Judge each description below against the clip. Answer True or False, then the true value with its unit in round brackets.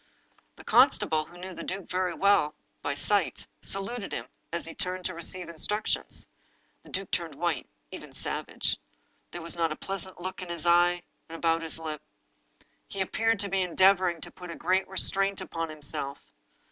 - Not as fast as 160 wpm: False (175 wpm)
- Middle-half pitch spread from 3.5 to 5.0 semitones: False (2.5 semitones)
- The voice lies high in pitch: False (175 Hz)